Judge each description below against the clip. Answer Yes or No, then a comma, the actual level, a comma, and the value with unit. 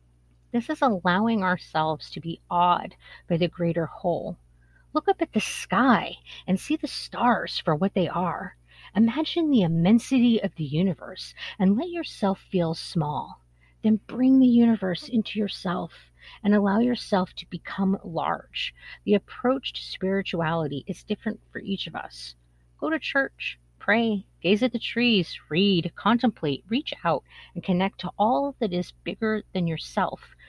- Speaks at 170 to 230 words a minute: No, average, 155 wpm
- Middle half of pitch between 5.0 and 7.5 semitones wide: Yes, wide, 5.4 semitones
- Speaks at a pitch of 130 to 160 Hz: No, high, 195 Hz